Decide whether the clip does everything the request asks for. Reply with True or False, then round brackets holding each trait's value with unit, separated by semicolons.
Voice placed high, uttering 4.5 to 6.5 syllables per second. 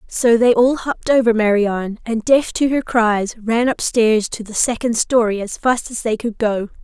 True (230 Hz; 4.6 syllables/s)